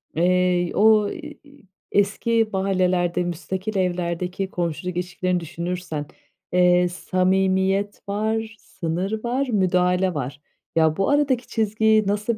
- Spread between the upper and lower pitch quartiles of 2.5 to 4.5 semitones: Yes, average, 3.1 semitones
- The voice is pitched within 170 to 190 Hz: Yes, medium, 185 Hz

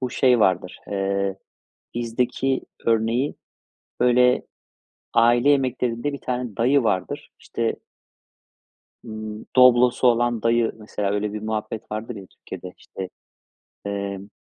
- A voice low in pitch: Yes, low, 115 Hz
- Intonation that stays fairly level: No, average, 3.2 semitones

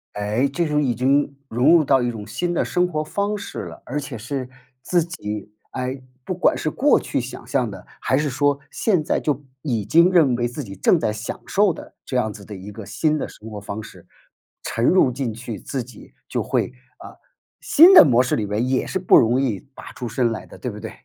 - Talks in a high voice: No, low, 130 Hz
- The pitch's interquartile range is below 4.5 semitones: No, wide, 5.5 semitones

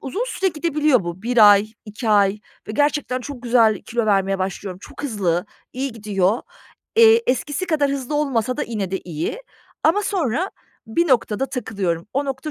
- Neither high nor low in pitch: No, high, 245 Hz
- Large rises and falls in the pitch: Yes, wide, 6.2 semitones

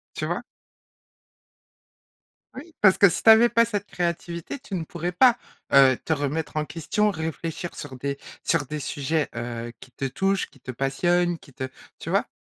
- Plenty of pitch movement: Yes, wide, 5.8 semitones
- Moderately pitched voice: Yes, medium, 165 Hz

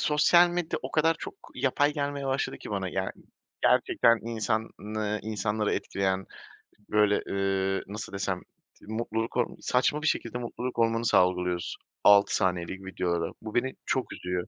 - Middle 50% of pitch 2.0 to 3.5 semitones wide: No, average, 4.6 semitones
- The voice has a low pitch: Yes, low, 110 Hz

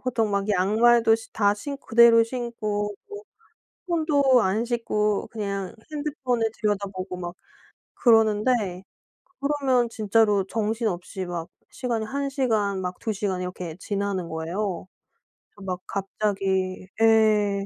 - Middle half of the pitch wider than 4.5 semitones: No, average, 3.3 semitones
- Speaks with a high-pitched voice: Yes, high, 210 Hz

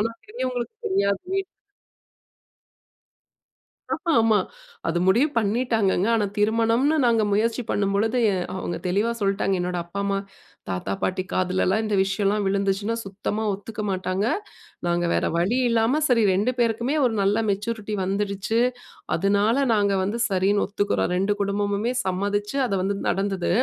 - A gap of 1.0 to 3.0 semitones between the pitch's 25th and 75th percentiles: Yes, narrow, 2.6 semitones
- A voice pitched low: No, high, 205 Hz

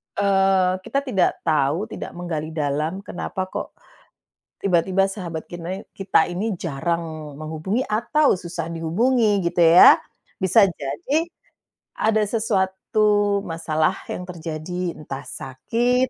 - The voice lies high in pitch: No, medium, 180 Hz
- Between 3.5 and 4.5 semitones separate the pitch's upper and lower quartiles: Yes, average, 4.0 semitones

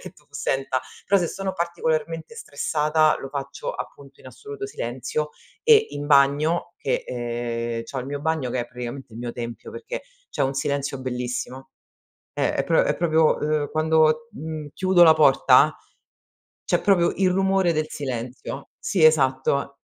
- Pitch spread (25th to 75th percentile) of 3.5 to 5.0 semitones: Yes, average, 4.3 semitones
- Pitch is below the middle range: No, medium, 150 Hz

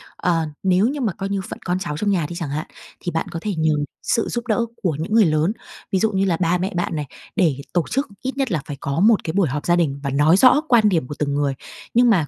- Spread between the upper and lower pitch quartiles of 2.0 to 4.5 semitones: No, average, 5.3 semitones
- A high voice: No, medium, 180 Hz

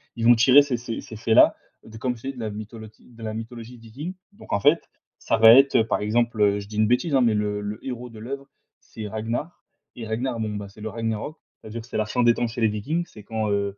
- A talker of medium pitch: No, low, 115 Hz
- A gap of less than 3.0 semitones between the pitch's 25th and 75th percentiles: Yes, narrow, 2.4 semitones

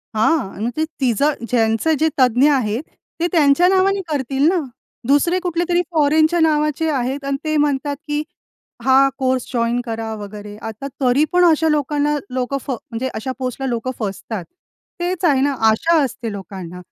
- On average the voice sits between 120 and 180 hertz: No, very high, 275 Hz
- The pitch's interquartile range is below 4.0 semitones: No, average, 5.0 semitones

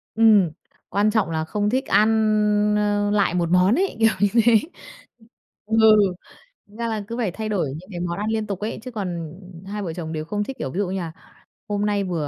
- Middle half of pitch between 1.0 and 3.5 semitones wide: Yes, average, 3.1 semitones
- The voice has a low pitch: No, high, 205 Hz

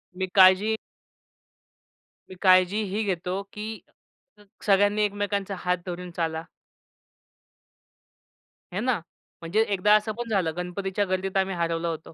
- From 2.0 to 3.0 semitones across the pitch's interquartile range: Yes, narrow, 2.4 semitones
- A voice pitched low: No, high, 190 Hz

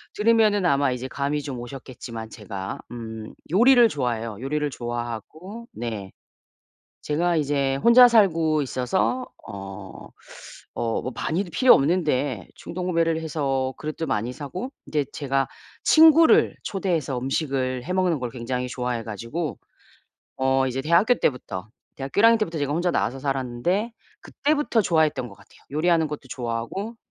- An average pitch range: No, wide, 6.1 semitones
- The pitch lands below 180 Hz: Yes, medium, 140 Hz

